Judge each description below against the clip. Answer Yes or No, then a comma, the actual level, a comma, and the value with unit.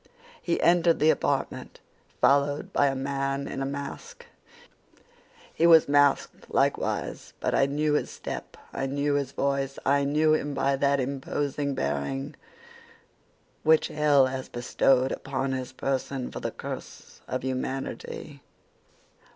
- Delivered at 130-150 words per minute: Yes, slow, 135 wpm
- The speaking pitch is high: No, medium, 140 Hz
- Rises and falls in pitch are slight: Yes, narrow, 1.5 semitones